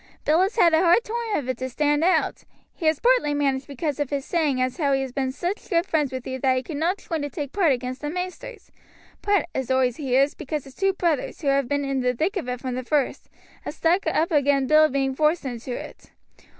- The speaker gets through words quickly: Yes, fast, 240 wpm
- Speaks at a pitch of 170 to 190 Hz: No, very high, 290 Hz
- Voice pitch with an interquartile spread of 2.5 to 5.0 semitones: Yes, average, 4.2 semitones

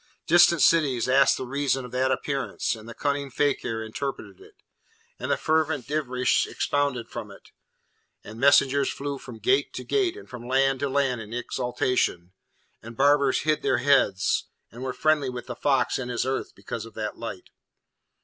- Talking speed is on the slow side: No, average, 175 wpm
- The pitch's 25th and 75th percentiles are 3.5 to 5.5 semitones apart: No, average, 2.9 semitones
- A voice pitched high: No, low, 130 Hz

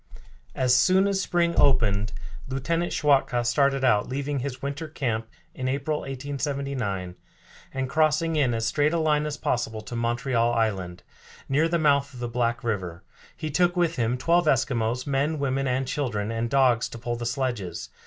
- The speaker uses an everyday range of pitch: Yes, average, 3.9 semitones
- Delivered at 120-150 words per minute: No, average, 170 wpm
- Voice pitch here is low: Yes, low, 130 Hz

